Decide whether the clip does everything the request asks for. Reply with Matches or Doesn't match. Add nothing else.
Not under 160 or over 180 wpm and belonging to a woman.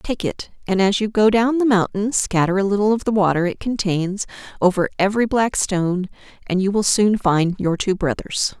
Doesn't match